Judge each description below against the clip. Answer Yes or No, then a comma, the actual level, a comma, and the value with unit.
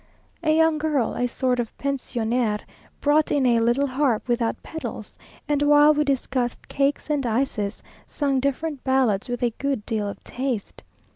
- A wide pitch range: No, average, 3.5 semitones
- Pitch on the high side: Yes, very high, 265 Hz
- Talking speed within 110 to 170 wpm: Yes, average, 160 wpm